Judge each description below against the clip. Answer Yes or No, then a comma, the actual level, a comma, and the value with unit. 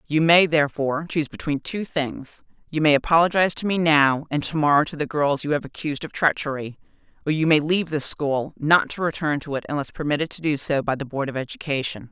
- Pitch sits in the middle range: Yes, medium, 150 Hz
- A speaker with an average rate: No, fast, 225 wpm